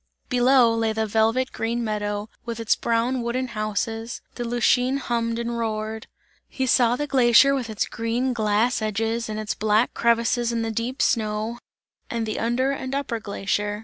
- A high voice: Yes, high, 230 Hz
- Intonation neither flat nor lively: No, narrow, 1.8 semitones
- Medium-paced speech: Yes, average, 170 wpm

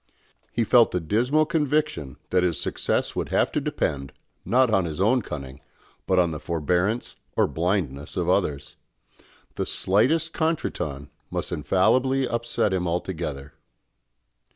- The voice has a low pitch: Yes, very low, 95 Hz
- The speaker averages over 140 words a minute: No, slow, 135 wpm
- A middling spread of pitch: No, wide, 8.1 semitones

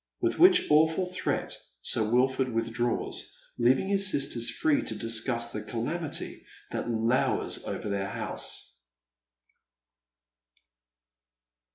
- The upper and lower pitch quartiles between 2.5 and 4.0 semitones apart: No, wide, 5.4 semitones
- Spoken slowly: Yes, slow, 100 wpm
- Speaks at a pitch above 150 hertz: No, low, 120 Hz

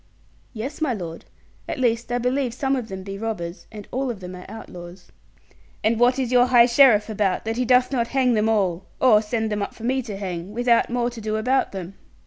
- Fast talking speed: Yes, fast, 225 wpm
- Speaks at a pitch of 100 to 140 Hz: No, high, 225 Hz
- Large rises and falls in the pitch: No, average, 3.7 semitones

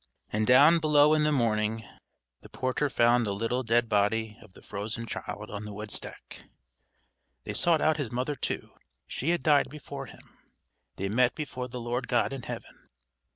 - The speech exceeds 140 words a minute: Yes, average, 175 wpm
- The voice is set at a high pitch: No, low, 120 Hz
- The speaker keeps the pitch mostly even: No, average, 5.0 semitones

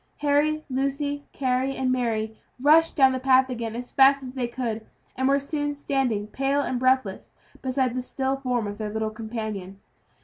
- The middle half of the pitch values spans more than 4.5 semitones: No, average, 3.1 semitones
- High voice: Yes, very high, 260 Hz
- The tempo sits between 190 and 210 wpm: No, average, 175 wpm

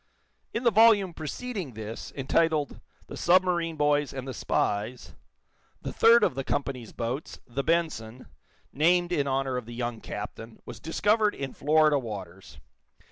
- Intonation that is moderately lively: No, wide, 6.1 semitones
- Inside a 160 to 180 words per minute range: No, average, 145 wpm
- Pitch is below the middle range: No, medium, 145 Hz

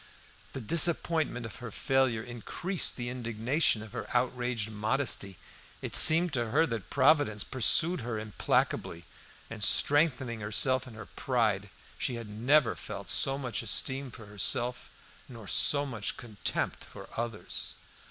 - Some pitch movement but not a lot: Yes, average, 3.7 semitones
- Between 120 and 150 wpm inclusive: Yes, average, 140 wpm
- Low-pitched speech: Yes, low, 120 Hz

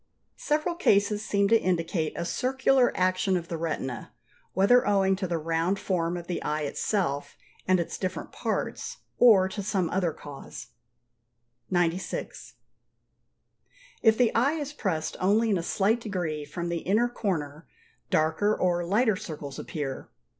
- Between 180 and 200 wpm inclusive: No, average, 145 wpm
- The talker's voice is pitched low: No, medium, 185 Hz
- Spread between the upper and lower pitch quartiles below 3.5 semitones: No, average, 4.3 semitones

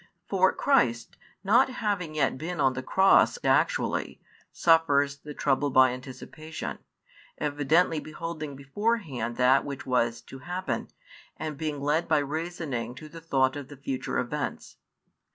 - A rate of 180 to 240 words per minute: No, slow, 135 wpm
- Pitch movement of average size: Yes, average, 3.9 semitones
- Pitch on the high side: No, medium, 145 Hz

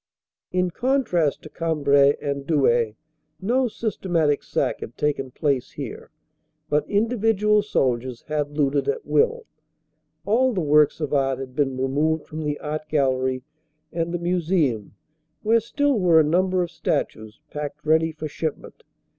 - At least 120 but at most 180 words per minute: Yes, average, 145 wpm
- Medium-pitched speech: Yes, medium, 155 Hz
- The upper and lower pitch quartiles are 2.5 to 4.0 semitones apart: No, average, 4.9 semitones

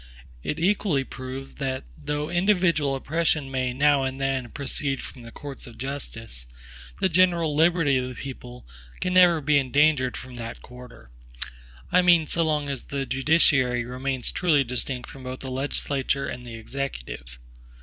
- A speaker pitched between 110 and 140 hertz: Yes, low, 135 Hz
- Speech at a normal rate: Yes, average, 160 wpm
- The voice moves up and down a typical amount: Yes, average, 3.2 semitones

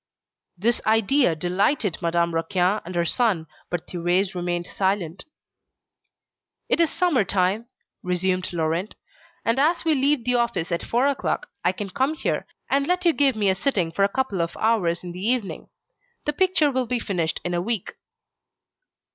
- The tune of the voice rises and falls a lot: Yes, wide, 6.6 semitones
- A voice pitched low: No, high, 200 Hz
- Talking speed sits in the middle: Yes, average, 170 wpm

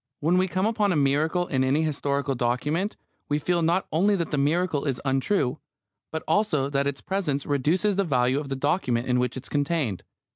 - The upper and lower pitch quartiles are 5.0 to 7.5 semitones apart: No, average, 4.6 semitones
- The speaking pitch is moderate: Yes, medium, 145 Hz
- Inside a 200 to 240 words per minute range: Yes, fast, 205 wpm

